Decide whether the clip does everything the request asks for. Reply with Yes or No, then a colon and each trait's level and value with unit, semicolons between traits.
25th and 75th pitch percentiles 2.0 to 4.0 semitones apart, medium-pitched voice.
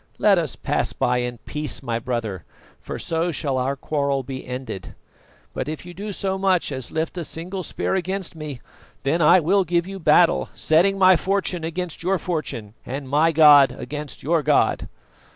No: average, 4.8 semitones; medium, 160 Hz